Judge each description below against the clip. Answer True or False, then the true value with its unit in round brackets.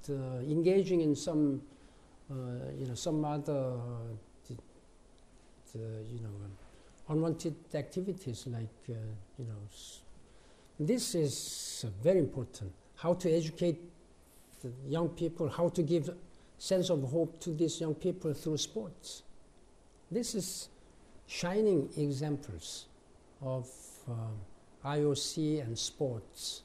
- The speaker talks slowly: True (125 wpm)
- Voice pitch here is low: False (145 Hz)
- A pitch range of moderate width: False (6.3 semitones)